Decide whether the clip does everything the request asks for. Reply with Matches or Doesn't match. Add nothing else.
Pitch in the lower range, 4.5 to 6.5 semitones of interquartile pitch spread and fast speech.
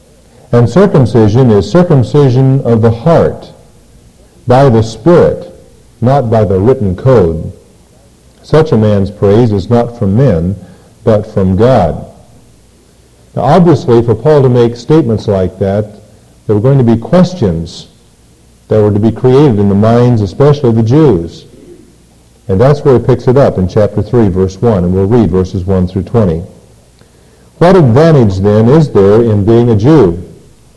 Doesn't match